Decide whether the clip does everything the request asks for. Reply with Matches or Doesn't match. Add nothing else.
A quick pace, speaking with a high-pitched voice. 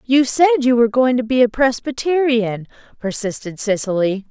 Doesn't match